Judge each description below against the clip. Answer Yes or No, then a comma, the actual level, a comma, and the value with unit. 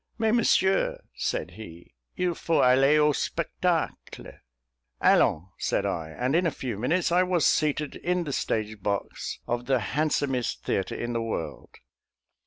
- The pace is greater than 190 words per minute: No, average, 150 wpm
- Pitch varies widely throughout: Yes, wide, 7.3 semitones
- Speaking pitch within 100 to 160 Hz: Yes, low, 135 Hz